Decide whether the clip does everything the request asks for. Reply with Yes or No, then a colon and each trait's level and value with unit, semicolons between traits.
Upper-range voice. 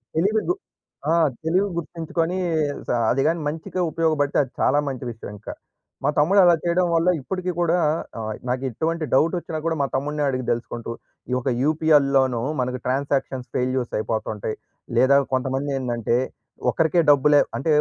No: medium, 145 Hz